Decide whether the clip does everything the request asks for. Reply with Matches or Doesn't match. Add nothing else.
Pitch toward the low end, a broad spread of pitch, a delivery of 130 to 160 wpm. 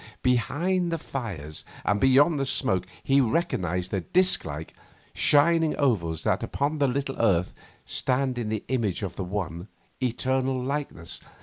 Matches